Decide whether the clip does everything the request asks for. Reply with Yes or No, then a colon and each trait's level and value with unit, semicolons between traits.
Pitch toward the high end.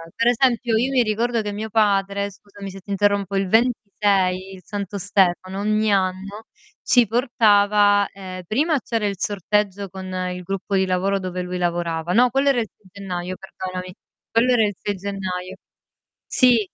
Yes: high, 200 Hz